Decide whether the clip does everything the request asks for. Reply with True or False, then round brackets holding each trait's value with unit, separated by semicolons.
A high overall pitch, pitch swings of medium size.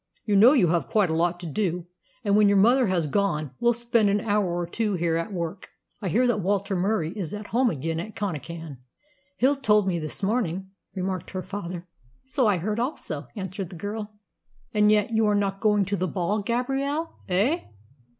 True (200 Hz; 3.8 semitones)